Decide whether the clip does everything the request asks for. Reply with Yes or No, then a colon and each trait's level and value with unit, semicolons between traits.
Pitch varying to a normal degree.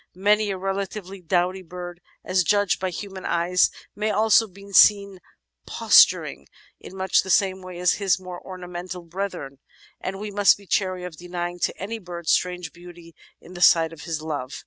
No: narrow, 2.0 semitones